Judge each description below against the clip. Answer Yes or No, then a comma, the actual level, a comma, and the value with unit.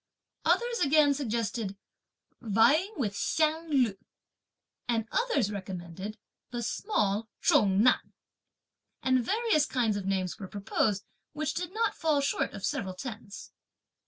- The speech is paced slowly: Yes, slow, 130 wpm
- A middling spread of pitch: No, wide, 7.1 semitones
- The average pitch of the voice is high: Yes, high, 235 Hz